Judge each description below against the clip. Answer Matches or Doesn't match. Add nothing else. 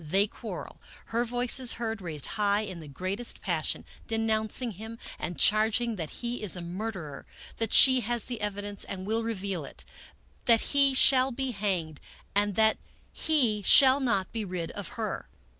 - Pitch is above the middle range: Matches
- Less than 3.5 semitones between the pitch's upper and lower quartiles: Doesn't match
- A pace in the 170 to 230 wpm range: Matches